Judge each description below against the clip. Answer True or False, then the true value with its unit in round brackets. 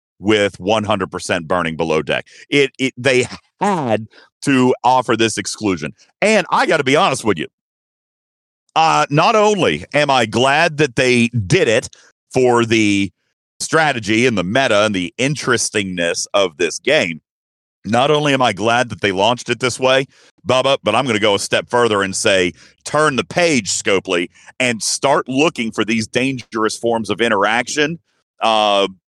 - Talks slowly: False (165 wpm)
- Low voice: True (115 Hz)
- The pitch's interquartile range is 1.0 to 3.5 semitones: False (4.1 semitones)